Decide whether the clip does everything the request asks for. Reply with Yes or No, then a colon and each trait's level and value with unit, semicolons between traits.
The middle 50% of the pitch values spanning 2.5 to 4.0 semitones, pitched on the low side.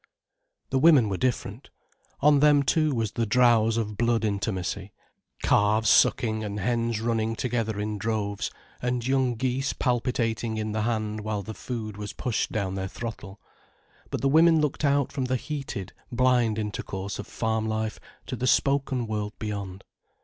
Yes: average, 3.2 semitones; low, 115 Hz